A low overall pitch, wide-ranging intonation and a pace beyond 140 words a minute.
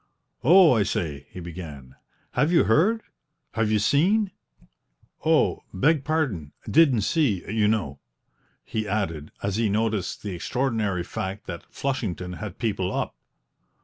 No: low, 105 Hz; wide, 7.0 semitones; slow, 135 wpm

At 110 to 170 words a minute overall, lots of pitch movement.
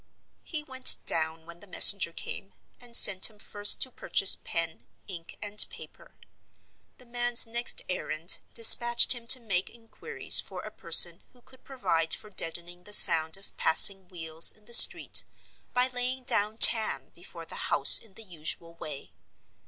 Yes: average, 160 wpm; wide, 6.0 semitones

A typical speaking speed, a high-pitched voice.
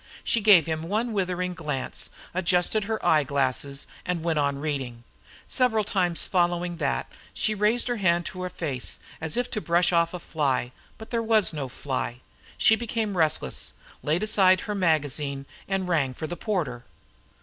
No: average, 170 wpm; medium, 175 Hz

